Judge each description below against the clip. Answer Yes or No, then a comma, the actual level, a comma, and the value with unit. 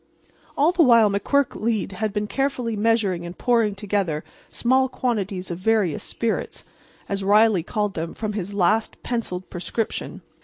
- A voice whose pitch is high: Yes, high, 210 Hz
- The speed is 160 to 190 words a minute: No, average, 145 wpm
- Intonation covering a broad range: No, average, 3.3 semitones